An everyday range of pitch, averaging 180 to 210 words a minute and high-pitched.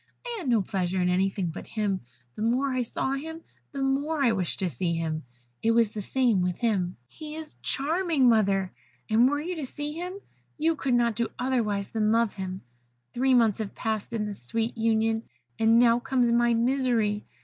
Yes: average, 4.7 semitones; average, 195 wpm; high, 230 Hz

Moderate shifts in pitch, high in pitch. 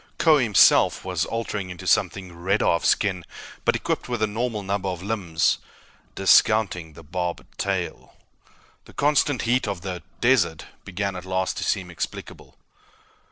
No: average, 3.7 semitones; very low, 95 Hz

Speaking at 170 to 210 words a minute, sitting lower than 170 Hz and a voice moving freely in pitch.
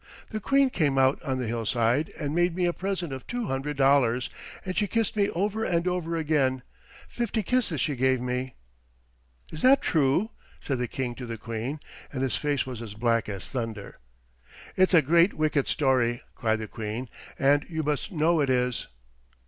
Yes: average, 185 wpm; medium, 140 Hz; wide, 5.7 semitones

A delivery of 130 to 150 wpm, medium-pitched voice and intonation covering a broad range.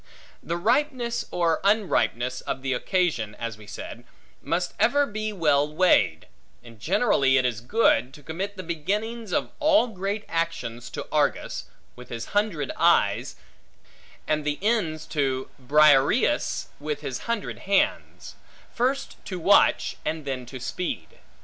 Yes: average, 140 wpm; medium, 165 Hz; wide, 7.9 semitones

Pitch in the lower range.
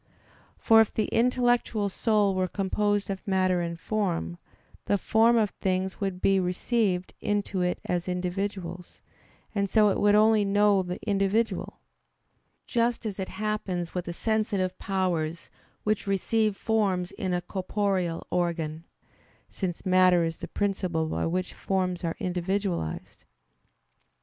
No: high, 190 Hz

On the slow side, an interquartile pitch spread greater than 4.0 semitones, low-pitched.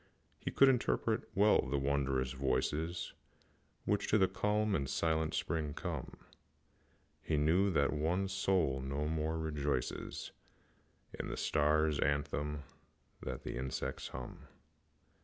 Yes: slow, 125 wpm; average, 4.4 semitones; very low, 75 Hz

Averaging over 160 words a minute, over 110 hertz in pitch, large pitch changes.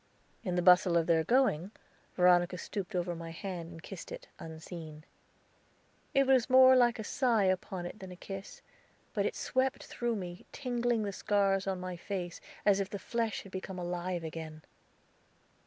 No: average, 170 wpm; high, 190 Hz; average, 4.2 semitones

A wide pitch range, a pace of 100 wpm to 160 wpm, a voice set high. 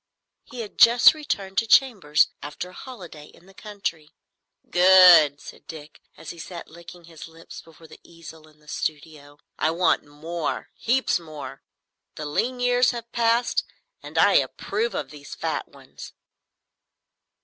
No: wide, 6.6 semitones; average, 150 wpm; medium, 170 Hz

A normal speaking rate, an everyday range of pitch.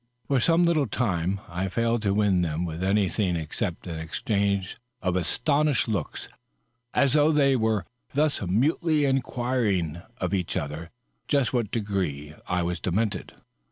No: average, 150 wpm; wide, 6.4 semitones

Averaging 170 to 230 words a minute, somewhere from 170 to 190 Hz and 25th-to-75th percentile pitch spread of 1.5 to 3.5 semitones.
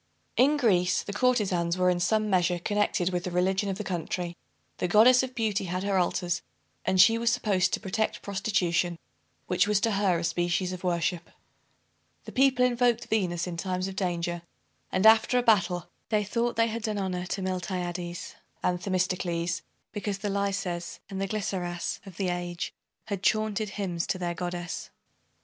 Yes: average, 175 wpm; medium, 185 Hz; average, 3.1 semitones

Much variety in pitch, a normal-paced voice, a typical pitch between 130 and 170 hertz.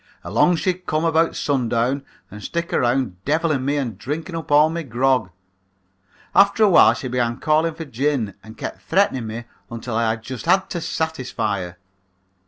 Yes: wide, 5.7 semitones; average, 175 wpm; low, 135 Hz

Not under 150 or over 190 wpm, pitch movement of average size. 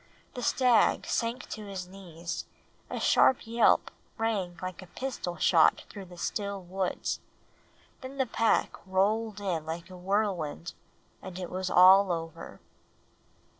No: slow, 135 wpm; average, 3.6 semitones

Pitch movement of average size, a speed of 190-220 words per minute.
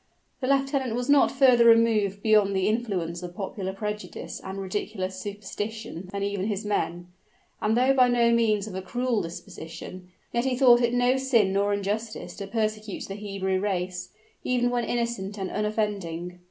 No: average, 3.6 semitones; average, 165 wpm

